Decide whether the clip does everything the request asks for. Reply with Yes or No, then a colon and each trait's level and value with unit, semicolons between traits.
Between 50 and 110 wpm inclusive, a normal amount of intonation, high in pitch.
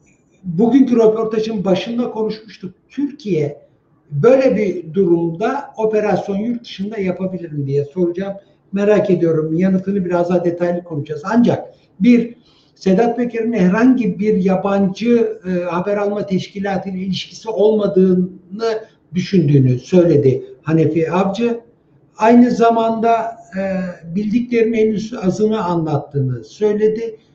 Yes: average, 105 wpm; average, 4.2 semitones; high, 195 Hz